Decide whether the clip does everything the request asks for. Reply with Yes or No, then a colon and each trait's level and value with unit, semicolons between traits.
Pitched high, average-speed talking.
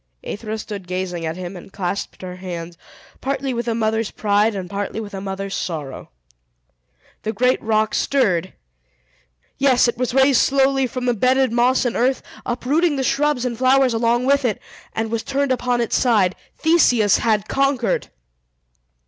Yes: high, 230 Hz; average, 165 wpm